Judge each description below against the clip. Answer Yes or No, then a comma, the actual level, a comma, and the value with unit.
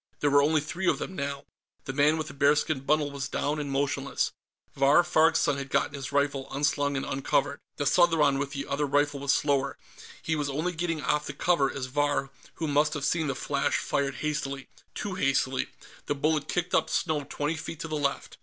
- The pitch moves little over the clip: Yes, narrow, 1.9 semitones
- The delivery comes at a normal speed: No, fast, 210 wpm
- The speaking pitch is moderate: Yes, medium, 145 Hz